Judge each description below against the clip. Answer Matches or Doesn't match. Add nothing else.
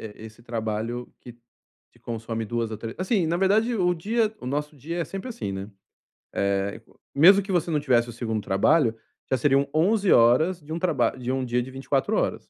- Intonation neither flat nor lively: Doesn't match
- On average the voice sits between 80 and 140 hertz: Matches